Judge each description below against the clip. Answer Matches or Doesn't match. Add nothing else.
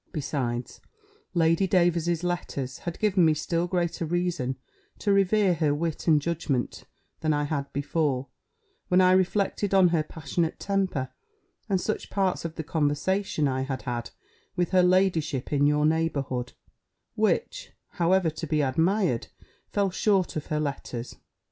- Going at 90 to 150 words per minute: Matches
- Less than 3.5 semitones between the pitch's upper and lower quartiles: Doesn't match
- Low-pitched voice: Doesn't match